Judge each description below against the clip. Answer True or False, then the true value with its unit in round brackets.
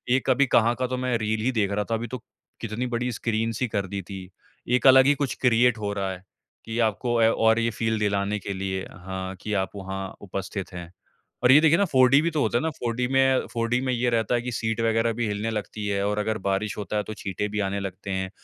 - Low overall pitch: True (110 Hz)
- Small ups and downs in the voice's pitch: False (3.5 semitones)